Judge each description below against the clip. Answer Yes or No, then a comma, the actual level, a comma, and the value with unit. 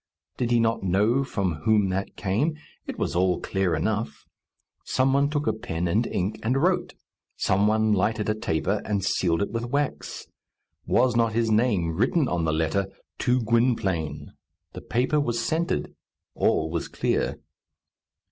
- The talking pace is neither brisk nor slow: Yes, average, 160 wpm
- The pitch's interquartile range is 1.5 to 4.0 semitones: No, average, 4.5 semitones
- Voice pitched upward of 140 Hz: No, low, 110 Hz